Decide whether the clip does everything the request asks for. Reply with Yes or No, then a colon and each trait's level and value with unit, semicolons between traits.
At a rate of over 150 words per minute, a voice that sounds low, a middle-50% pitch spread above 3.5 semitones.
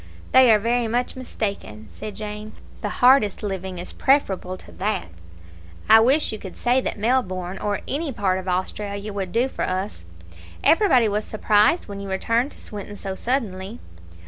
No: average, 170 wpm; high, 210 Hz; average, 4.1 semitones